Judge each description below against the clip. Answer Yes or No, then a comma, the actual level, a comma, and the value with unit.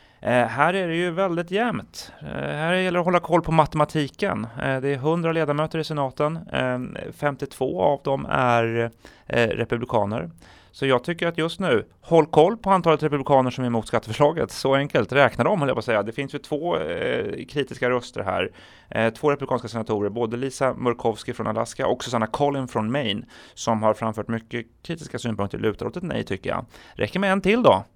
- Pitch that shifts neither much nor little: No, wide, 5.7 semitones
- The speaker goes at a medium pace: No, fast, 200 wpm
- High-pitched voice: No, low, 135 Hz